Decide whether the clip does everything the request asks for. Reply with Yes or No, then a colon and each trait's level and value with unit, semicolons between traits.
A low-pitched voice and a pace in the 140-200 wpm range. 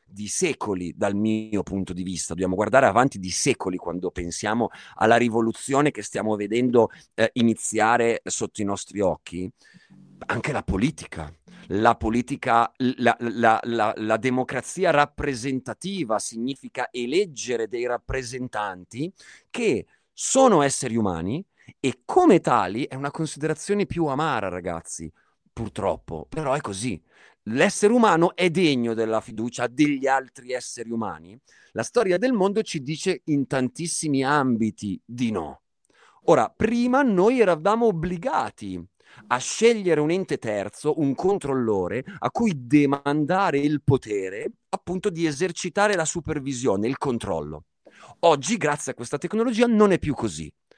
No: low, 130 Hz; average, 130 wpm